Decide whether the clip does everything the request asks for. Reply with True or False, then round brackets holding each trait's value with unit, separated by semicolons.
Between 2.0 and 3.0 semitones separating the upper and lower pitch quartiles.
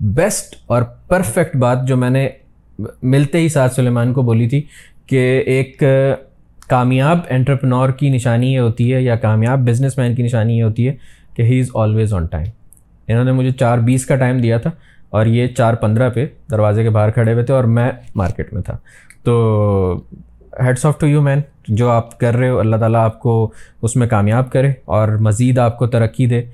True (2.6 semitones)